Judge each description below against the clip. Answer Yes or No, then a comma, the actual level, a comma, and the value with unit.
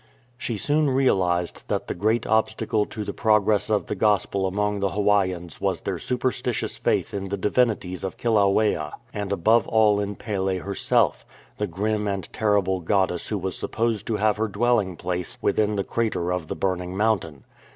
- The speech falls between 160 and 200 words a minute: Yes, average, 175 wpm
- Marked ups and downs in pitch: No, average, 2.7 semitones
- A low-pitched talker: Yes, low, 105 Hz